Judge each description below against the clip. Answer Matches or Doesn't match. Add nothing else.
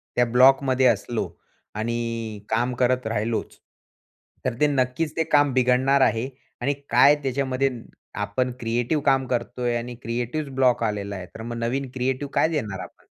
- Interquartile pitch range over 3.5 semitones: Doesn't match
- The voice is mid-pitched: Doesn't match